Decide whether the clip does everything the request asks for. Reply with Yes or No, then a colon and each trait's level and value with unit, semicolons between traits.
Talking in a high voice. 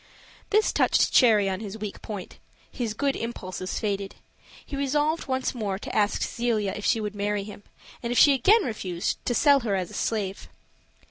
Yes: high, 215 Hz